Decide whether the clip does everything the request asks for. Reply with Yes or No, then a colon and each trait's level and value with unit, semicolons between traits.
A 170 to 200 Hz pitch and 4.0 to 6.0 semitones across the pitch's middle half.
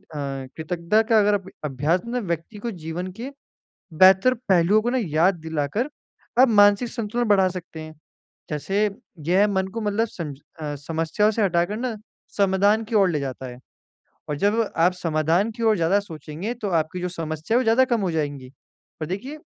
Yes: high, 190 Hz; average, 5.1 semitones